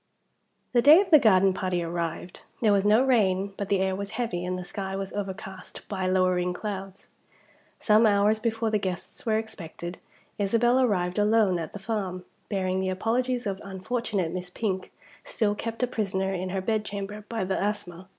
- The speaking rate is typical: Yes, average, 180 wpm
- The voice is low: No, high, 195 Hz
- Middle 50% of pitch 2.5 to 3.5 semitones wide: Yes, average, 2.9 semitones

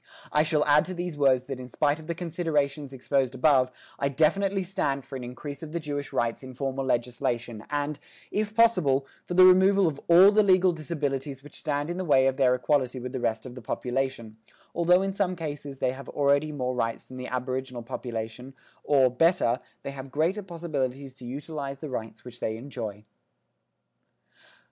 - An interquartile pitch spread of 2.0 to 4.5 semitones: Yes, average, 4.0 semitones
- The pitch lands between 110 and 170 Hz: Yes, medium, 140 Hz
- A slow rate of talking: No, average, 190 wpm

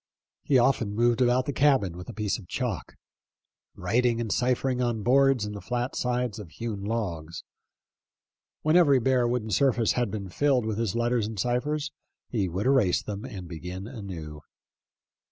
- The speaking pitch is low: Yes, low, 115 Hz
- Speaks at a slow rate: No, average, 170 wpm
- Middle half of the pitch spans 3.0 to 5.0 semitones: Yes, average, 4.0 semitones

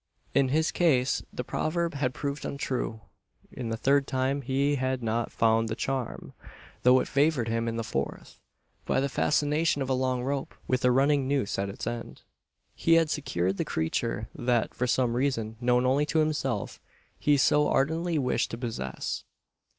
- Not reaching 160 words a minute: No, average, 175 wpm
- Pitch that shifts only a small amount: No, average, 3.4 semitones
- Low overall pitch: Yes, low, 130 Hz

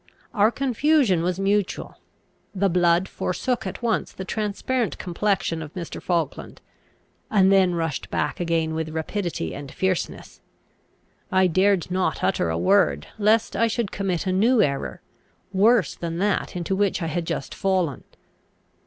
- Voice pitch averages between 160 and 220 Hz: Yes, medium, 185 Hz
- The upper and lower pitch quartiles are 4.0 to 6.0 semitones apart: No, average, 3.4 semitones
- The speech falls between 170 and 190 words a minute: No, average, 145 wpm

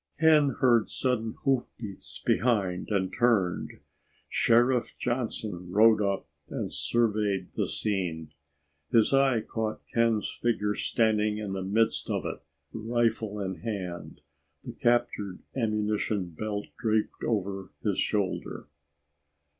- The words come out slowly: Yes, slow, 115 wpm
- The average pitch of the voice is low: Yes, low, 110 Hz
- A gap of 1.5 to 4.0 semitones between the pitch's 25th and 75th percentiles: Yes, average, 3.2 semitones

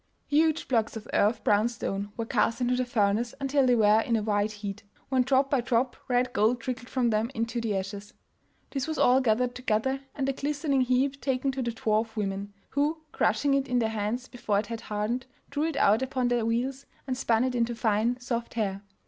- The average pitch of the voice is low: No, high, 240 Hz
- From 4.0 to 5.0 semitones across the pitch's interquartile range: No, average, 3.2 semitones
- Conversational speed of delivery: No, fast, 210 wpm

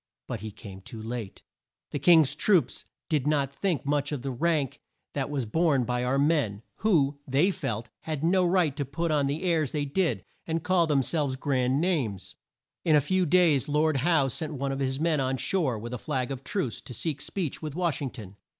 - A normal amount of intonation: Yes, average, 4.1 semitones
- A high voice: No, medium, 145 Hz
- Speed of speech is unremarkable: No, fast, 210 wpm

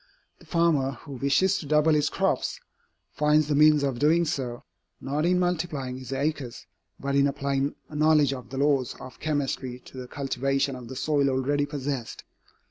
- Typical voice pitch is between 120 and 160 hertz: Yes, medium, 140 Hz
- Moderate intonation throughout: No, narrow, 2.3 semitones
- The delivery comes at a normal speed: Yes, average, 175 wpm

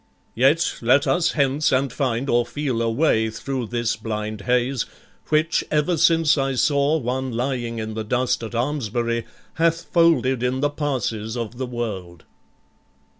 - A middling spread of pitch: Yes, average, 3.9 semitones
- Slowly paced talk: No, average, 155 wpm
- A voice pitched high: No, low, 125 Hz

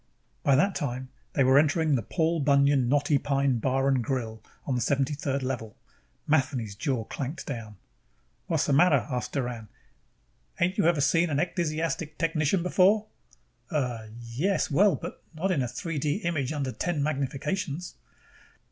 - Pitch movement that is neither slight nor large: Yes, average, 4.1 semitones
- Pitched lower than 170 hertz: Yes, medium, 140 Hz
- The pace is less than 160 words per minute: Yes, average, 150 wpm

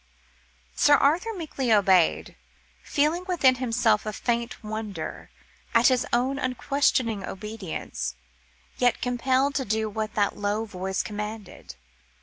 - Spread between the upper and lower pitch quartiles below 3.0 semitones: No, average, 3.7 semitones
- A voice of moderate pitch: No, high, 230 Hz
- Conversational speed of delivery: No, slow, 120 wpm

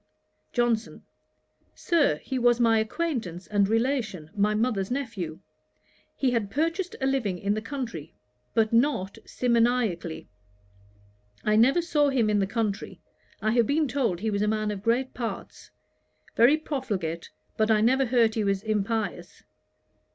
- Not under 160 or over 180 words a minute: No, average, 150 wpm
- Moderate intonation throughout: Yes, average, 3.9 semitones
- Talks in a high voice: Yes, high, 225 Hz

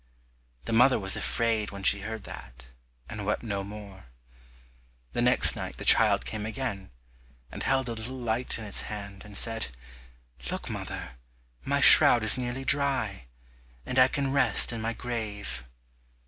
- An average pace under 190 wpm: Yes, average, 160 wpm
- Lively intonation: No, average, 3.4 semitones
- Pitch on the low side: Yes, low, 110 Hz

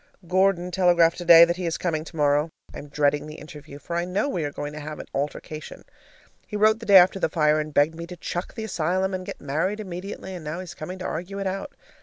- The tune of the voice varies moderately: Yes, average, 3.5 semitones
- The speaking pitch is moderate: Yes, medium, 170 Hz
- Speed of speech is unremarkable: No, fast, 245 wpm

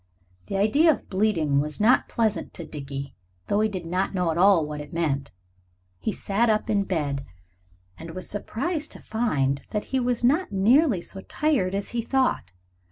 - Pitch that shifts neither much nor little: No, wide, 6.5 semitones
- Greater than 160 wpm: Yes, average, 180 wpm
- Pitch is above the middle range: Yes, high, 200 Hz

